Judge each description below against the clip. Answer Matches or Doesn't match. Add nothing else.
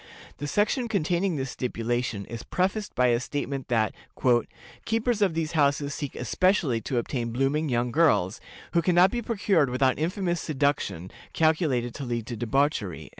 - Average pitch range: Doesn't match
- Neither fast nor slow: Matches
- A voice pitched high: Doesn't match